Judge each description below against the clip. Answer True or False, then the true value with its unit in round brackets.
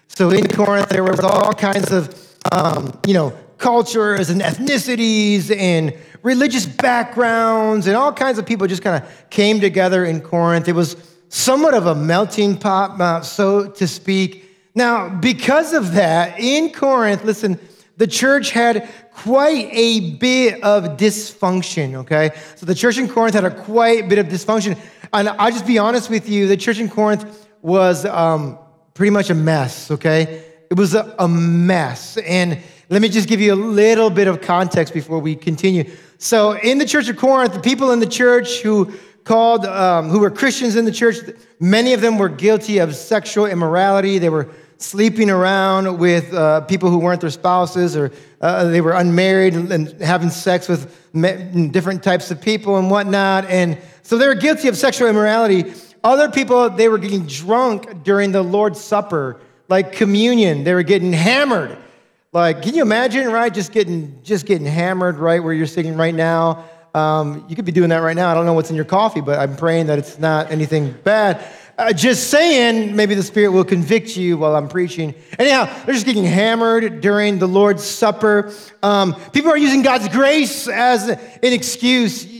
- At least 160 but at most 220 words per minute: True (185 wpm)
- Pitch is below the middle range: False (195 Hz)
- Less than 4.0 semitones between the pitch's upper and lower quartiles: False (4.6 semitones)